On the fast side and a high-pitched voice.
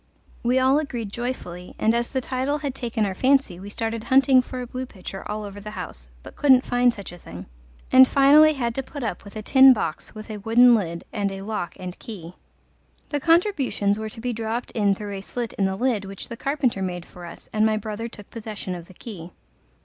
Yes: fast, 225 wpm; high, 225 Hz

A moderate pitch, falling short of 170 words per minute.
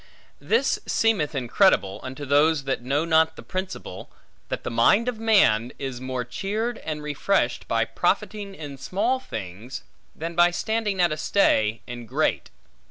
Yes: medium, 155 Hz; average, 155 wpm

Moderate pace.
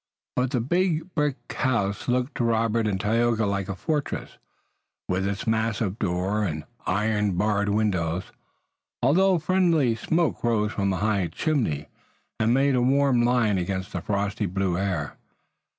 Yes: average, 150 wpm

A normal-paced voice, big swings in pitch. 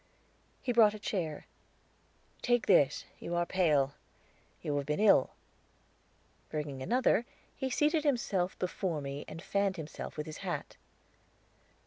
No: slow, 130 wpm; wide, 6.4 semitones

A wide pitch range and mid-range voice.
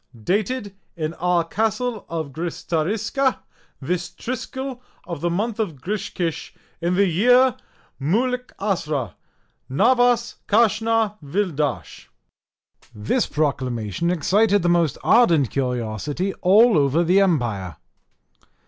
Yes: wide, 6.7 semitones; medium, 180 Hz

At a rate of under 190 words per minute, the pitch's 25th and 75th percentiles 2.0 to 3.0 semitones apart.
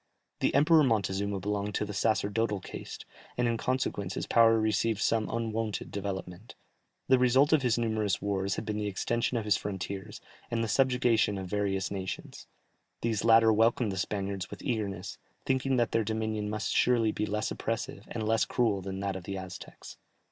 Yes: average, 175 wpm; narrow, 2.6 semitones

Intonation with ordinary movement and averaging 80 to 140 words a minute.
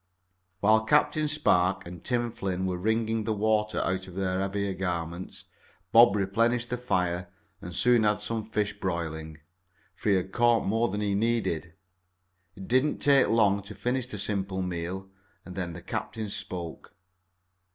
No: average, 3.6 semitones; average, 160 wpm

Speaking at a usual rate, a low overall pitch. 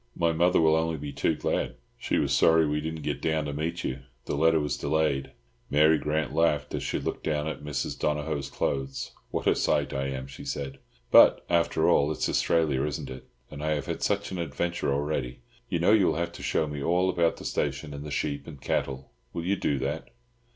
No: fast, 220 wpm; very low, 75 Hz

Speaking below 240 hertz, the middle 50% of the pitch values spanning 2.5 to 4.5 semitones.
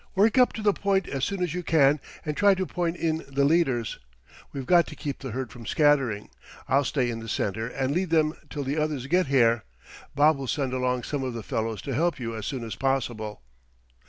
No: medium, 140 Hz; average, 5.1 semitones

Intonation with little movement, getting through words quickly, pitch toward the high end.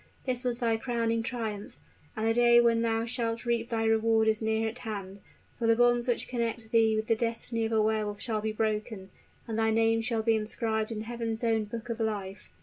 Yes: narrow, 1.1 semitones; fast, 220 wpm; high, 225 Hz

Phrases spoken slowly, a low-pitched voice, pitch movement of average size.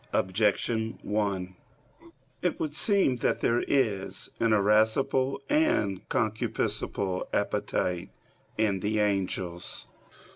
Yes: slow, 100 wpm; low, 105 Hz; average, 3.6 semitones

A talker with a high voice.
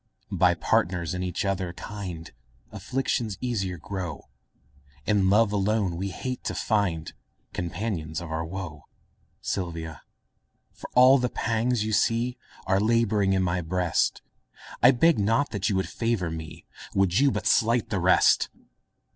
No: very low, 95 Hz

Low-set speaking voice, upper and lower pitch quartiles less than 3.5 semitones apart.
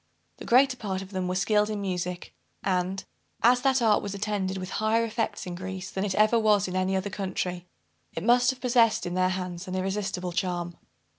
No: high, 190 Hz; average, 2.8 semitones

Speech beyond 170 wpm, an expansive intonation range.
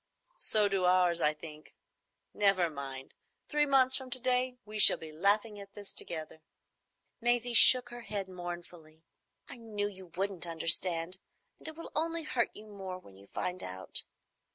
No: average, 165 wpm; wide, 6.1 semitones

